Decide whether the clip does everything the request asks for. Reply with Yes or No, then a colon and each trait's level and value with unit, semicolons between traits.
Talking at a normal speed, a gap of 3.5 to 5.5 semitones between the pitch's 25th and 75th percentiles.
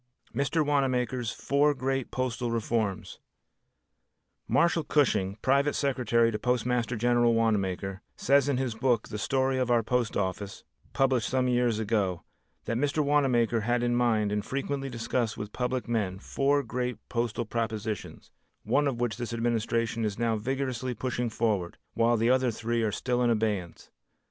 No: average, 155 wpm; narrow, 2.6 semitones